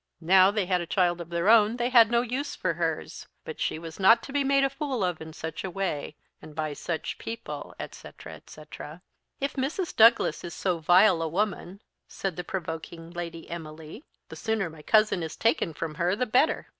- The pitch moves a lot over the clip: Yes, wide, 5.7 semitones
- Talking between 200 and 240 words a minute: Yes, fast, 205 wpm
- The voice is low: No, medium, 185 Hz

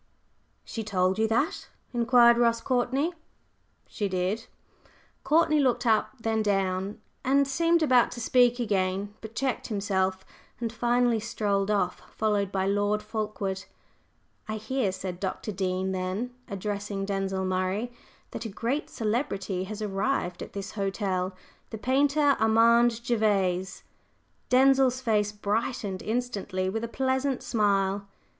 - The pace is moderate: No, slow, 130 wpm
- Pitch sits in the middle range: No, high, 215 Hz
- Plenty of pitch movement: No, average, 3.8 semitones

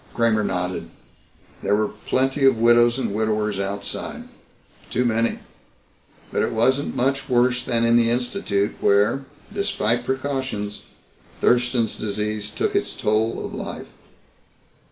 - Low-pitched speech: Yes, low, 115 Hz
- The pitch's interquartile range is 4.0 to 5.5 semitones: No, average, 3.0 semitones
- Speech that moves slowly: Yes, slow, 125 wpm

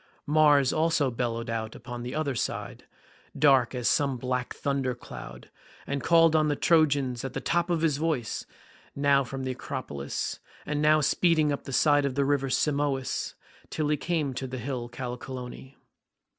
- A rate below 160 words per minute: No, average, 170 wpm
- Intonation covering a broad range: No, average, 3.0 semitones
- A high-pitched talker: No, medium, 140 Hz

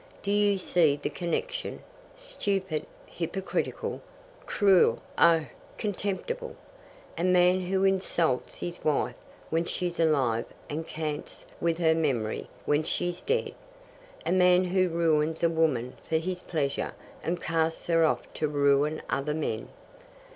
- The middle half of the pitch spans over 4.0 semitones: No, average, 3.3 semitones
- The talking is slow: Yes, slow, 130 wpm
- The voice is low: No, medium, 165 Hz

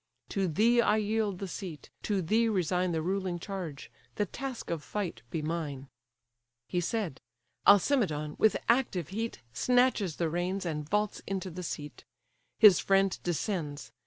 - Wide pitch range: No, average, 4.4 semitones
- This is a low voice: No, medium, 185 Hz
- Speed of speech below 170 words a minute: Yes, average, 150 wpm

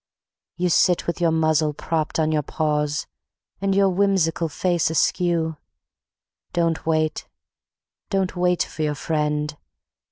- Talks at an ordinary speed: No, slow, 125 wpm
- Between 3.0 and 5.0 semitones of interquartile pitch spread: No, narrow, 2.5 semitones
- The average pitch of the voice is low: No, medium, 160 Hz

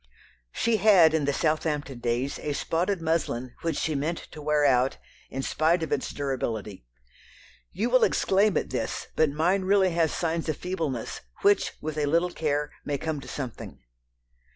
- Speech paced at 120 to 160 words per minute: No, average, 170 wpm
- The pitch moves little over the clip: No, average, 3.4 semitones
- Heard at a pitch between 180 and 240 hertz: No, medium, 155 Hz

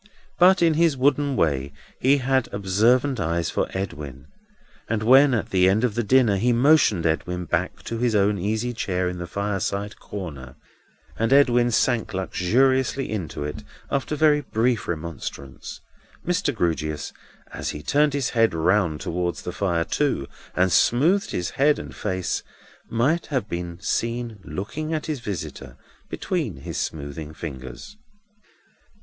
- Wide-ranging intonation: Yes, wide, 7.3 semitones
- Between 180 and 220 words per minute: No, average, 145 wpm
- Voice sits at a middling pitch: No, low, 105 Hz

